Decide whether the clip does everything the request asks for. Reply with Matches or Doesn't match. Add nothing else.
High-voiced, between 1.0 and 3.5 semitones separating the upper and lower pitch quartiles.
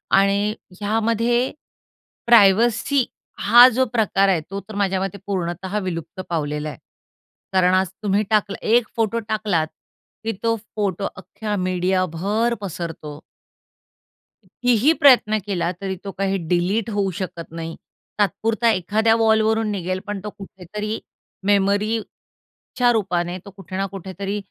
Matches